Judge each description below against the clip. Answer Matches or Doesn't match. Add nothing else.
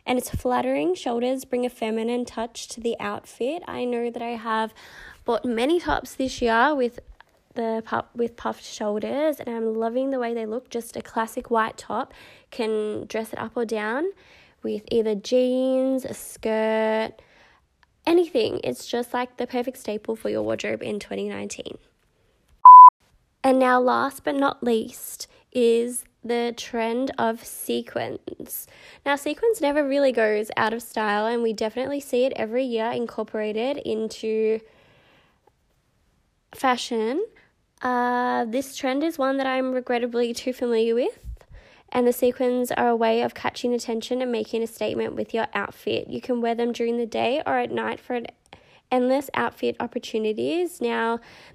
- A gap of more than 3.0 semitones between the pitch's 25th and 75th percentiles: Doesn't match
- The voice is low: Doesn't match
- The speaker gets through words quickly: Doesn't match